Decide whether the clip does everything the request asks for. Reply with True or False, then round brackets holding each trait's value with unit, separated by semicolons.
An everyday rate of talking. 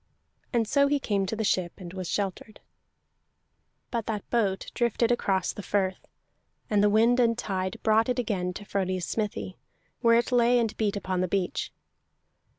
True (170 wpm)